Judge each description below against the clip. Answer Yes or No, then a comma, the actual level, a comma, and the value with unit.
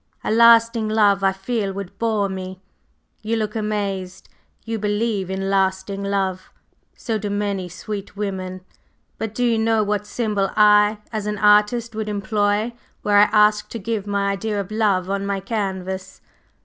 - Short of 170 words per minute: Yes, average, 160 wpm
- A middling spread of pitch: No, narrow, 1.8 semitones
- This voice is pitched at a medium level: No, high, 205 Hz